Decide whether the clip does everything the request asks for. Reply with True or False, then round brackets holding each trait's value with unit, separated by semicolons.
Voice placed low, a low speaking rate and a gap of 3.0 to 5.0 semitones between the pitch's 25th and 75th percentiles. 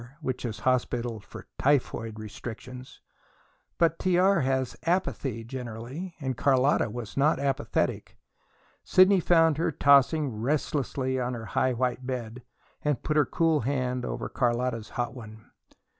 True (130 Hz; 130 wpm; 3.6 semitones)